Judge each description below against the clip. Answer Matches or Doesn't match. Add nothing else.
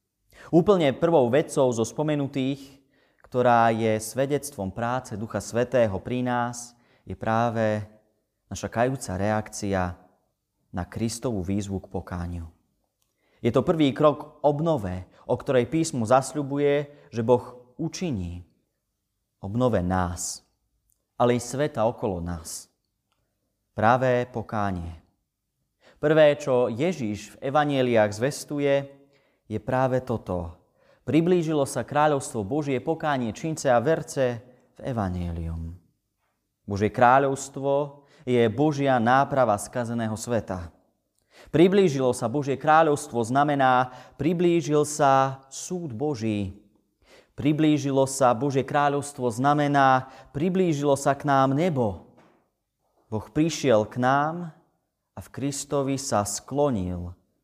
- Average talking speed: Doesn't match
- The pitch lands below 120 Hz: Doesn't match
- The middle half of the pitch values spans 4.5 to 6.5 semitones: Matches